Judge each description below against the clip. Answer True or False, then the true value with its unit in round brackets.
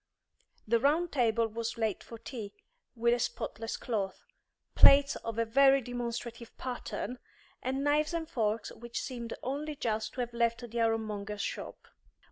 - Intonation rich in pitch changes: False (2.6 semitones)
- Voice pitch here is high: True (235 Hz)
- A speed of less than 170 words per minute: True (150 wpm)